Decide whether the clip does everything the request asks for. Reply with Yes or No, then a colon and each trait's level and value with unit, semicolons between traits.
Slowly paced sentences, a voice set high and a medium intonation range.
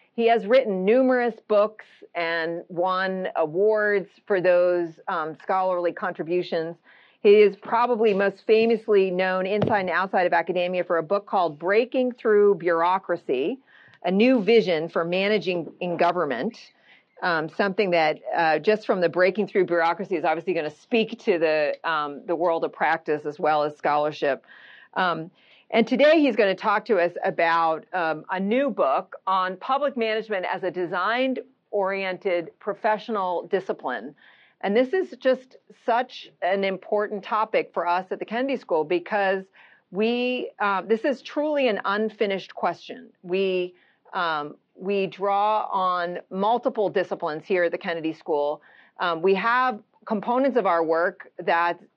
No: average, 150 wpm; high, 195 Hz; average, 4.3 semitones